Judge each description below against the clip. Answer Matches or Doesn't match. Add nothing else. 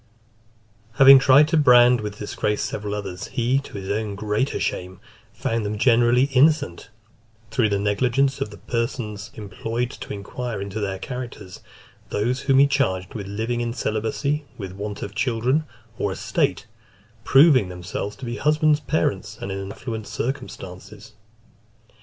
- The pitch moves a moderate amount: Matches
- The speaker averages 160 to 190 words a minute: Doesn't match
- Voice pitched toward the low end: Matches